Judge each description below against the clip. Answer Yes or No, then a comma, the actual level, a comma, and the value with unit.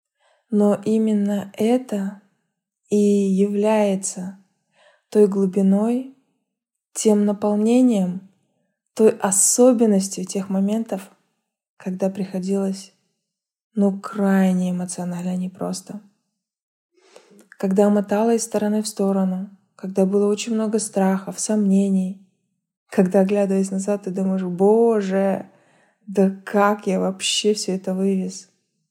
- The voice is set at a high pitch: Yes, high, 200 Hz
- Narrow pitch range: Yes, narrow, 1.5 semitones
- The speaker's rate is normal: No, slow, 95 wpm